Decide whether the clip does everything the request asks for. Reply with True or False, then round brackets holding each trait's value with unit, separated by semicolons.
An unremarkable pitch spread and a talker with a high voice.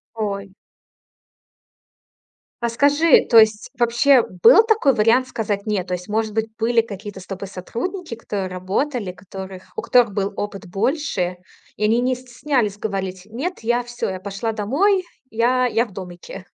True (4.1 semitones; 220 Hz)